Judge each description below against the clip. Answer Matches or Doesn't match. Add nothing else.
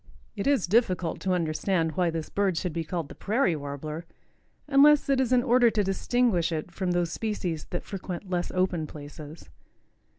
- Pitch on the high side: Doesn't match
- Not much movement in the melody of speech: Doesn't match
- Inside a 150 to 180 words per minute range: Matches